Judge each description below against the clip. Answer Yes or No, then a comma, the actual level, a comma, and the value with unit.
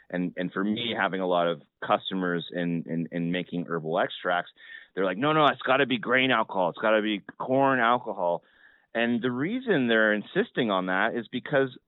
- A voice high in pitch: No, low, 110 Hz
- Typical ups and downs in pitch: No, wide, 6.3 semitones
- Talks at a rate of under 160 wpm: No, average, 200 wpm